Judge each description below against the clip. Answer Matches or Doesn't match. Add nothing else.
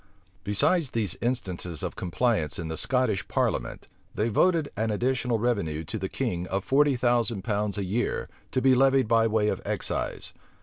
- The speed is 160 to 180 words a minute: Matches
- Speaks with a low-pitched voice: Matches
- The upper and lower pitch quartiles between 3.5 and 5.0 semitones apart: Matches